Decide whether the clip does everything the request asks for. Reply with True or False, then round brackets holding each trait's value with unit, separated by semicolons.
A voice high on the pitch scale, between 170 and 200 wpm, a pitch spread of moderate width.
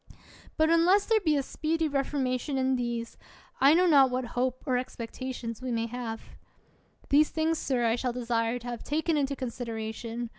True (255 Hz; 175 wpm; 3.8 semitones)